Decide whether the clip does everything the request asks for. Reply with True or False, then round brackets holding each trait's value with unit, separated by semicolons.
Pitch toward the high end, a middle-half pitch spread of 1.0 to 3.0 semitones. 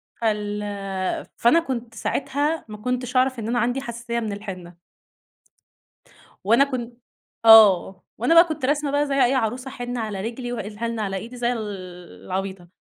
False (235 Hz; 3.4 semitones)